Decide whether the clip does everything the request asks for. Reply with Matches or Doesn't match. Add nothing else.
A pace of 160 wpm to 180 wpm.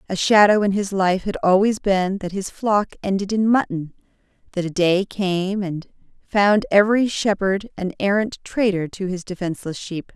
Matches